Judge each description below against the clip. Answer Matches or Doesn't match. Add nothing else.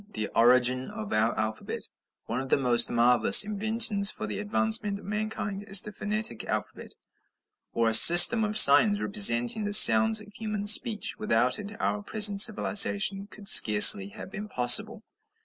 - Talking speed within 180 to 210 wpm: Doesn't match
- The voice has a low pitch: Doesn't match